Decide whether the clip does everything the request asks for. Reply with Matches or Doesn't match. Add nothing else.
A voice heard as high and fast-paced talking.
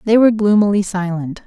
Doesn't match